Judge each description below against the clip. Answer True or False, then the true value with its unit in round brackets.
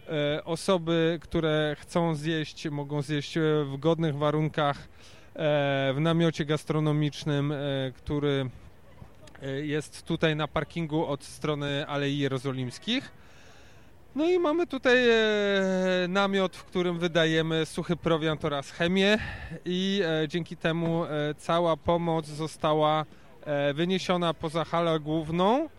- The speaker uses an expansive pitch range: False (2.7 semitones)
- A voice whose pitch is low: False (160 Hz)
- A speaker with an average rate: False (100 wpm)